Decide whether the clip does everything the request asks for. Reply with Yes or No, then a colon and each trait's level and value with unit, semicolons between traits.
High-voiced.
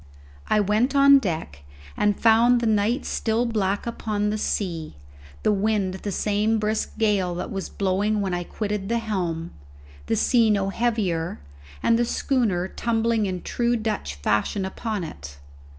Yes: high, 210 Hz